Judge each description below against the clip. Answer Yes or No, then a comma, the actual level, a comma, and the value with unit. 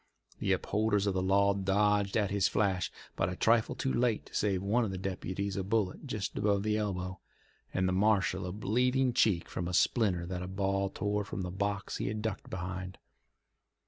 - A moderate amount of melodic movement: No, narrow, 2.2 semitones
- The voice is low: Yes, low, 100 Hz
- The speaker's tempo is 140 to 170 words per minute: No, average, 200 wpm